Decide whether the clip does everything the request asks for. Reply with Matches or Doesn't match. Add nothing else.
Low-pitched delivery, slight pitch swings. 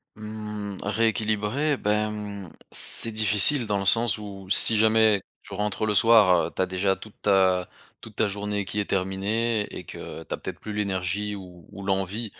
Matches